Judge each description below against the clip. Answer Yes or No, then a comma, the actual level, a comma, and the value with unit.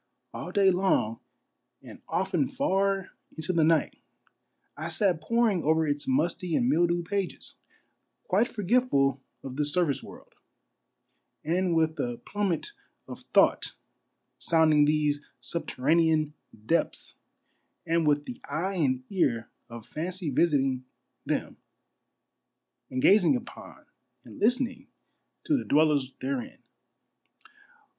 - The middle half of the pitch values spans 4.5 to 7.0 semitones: Yes, average, 4.9 semitones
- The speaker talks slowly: Yes, slow, 120 wpm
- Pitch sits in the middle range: Yes, medium, 165 Hz